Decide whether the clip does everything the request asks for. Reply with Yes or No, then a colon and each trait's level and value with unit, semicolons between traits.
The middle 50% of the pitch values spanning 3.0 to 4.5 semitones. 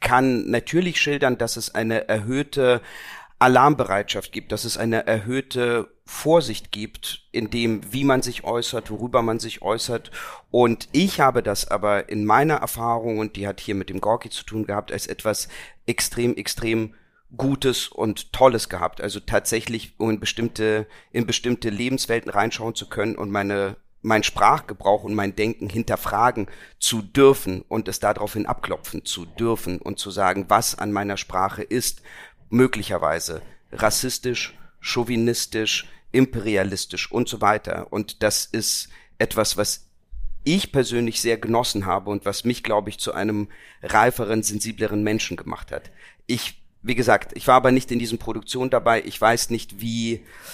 No: narrow, 2.5 semitones